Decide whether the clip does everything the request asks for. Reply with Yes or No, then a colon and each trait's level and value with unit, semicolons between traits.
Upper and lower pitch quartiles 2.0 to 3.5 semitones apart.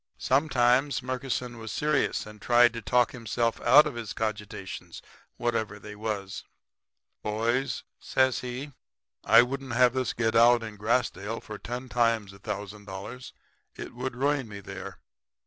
Yes: average, 2.9 semitones